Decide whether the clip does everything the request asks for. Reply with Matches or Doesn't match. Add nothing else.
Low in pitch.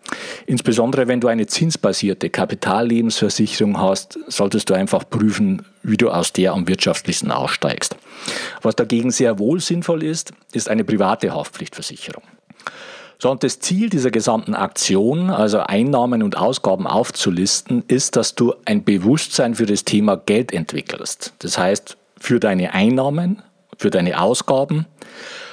Matches